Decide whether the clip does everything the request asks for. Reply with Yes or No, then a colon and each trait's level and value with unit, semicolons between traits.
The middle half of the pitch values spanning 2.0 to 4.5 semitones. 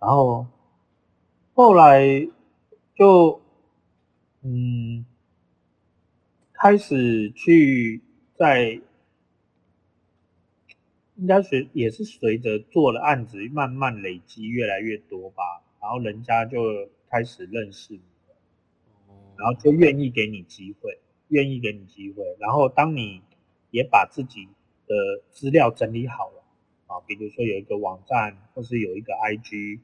No: average, 5.1 semitones